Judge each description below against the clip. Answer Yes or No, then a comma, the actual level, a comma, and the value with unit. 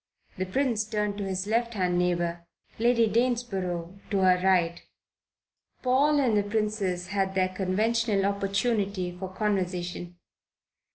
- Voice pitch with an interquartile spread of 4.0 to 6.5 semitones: No, average, 3.2 semitones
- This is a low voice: No, high, 195 Hz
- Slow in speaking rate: Yes, slow, 125 wpm